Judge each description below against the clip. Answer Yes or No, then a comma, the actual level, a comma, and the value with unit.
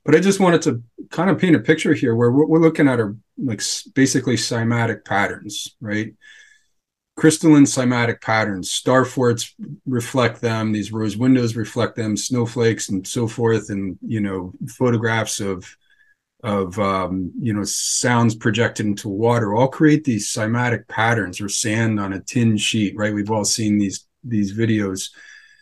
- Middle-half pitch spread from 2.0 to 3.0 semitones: No, average, 3.8 semitones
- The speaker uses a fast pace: No, average, 160 wpm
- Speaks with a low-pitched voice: Yes, low, 115 Hz